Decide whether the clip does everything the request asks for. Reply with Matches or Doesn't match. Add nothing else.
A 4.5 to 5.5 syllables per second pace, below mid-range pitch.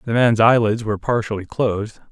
Doesn't match